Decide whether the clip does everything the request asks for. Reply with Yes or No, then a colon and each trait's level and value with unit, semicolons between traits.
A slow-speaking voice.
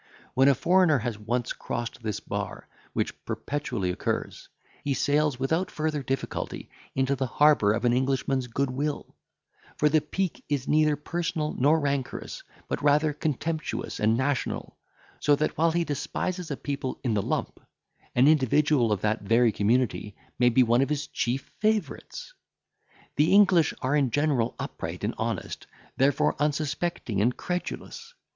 No: average, 150 wpm